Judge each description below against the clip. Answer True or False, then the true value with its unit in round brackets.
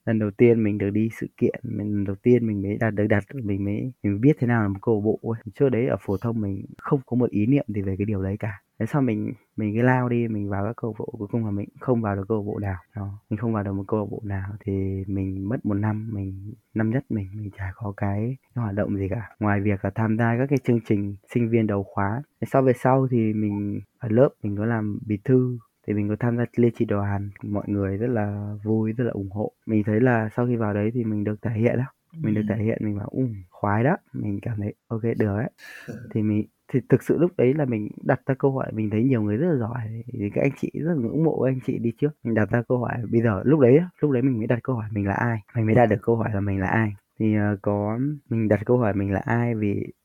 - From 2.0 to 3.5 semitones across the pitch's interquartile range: True (2.8 semitones)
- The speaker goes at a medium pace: False (285 wpm)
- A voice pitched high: False (110 Hz)